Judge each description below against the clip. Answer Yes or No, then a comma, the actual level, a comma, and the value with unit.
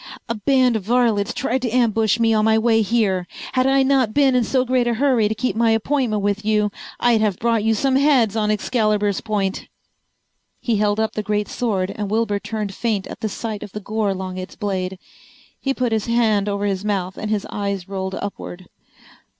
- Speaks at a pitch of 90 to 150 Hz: No, high, 215 Hz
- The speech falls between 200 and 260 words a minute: Yes, fast, 205 wpm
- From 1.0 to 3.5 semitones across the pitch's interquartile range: Yes, average, 2.7 semitones